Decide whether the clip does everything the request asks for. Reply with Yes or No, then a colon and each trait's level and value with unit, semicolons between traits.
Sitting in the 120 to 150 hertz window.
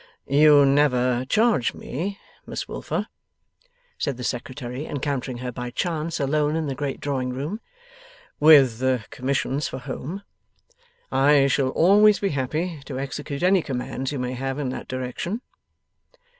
Yes: medium, 140 Hz